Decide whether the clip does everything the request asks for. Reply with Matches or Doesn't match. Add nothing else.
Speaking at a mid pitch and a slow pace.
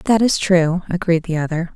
Doesn't match